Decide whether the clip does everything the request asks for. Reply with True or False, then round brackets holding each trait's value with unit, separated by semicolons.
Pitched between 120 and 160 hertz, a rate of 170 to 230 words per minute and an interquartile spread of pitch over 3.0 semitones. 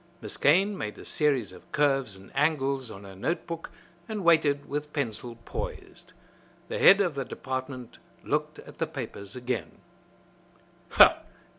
False (135 Hz; 145 wpm; 4.6 semitones)